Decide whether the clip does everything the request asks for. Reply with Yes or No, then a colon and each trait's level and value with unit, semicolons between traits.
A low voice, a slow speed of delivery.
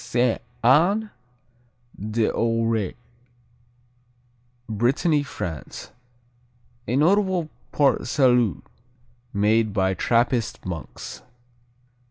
Yes: low, 115 Hz; slow, 65 wpm